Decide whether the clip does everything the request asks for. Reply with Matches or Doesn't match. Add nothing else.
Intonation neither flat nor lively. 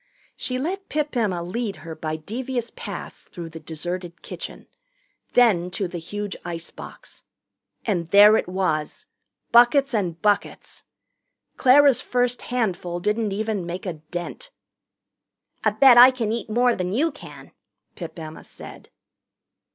Doesn't match